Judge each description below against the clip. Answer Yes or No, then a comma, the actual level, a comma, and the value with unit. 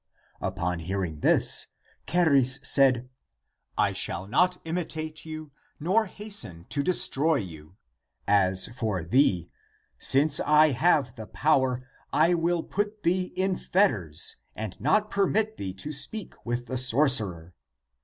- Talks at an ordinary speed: No, slow, 130 wpm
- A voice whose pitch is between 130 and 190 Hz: Yes, medium, 140 Hz